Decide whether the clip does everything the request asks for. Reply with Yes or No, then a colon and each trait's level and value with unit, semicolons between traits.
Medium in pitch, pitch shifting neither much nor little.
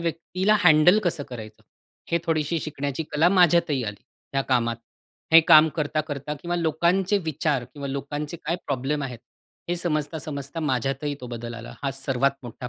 Yes: medium, 150 Hz; average, 3.6 semitones